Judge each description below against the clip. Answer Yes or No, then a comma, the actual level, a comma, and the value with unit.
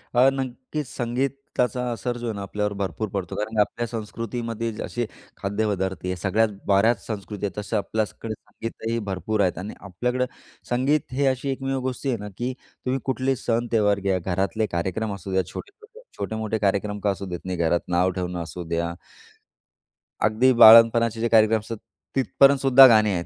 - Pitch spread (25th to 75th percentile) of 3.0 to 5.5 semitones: Yes, average, 3.9 semitones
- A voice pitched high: No, low, 110 Hz